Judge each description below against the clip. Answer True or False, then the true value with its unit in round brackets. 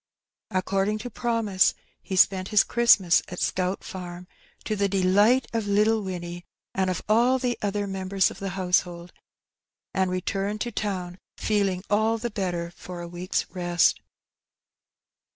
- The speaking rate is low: False (145 wpm)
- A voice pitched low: False (195 Hz)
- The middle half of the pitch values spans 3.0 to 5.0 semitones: False (2.6 semitones)